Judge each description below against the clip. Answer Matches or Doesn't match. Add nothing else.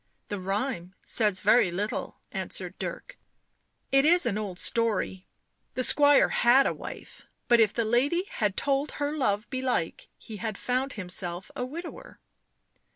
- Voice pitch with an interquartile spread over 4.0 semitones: Matches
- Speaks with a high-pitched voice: Matches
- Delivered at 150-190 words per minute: Matches